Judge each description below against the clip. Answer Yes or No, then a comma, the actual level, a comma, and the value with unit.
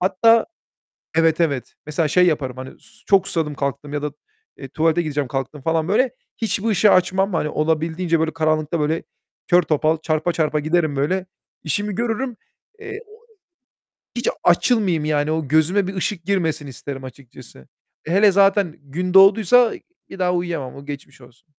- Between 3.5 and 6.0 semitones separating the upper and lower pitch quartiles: Yes, average, 4.3 semitones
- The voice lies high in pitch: No, medium, 160 Hz